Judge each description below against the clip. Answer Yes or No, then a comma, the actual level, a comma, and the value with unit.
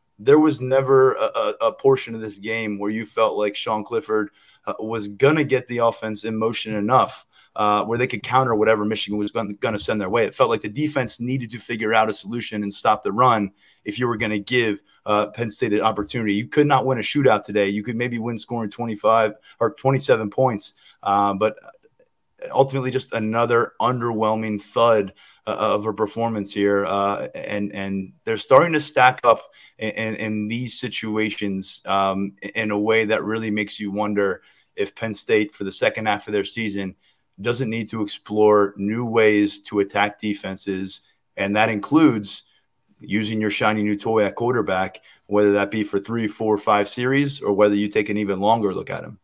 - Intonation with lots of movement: No, narrow, 2.5 semitones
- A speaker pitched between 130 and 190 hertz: No, low, 110 Hz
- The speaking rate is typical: Yes, average, 195 wpm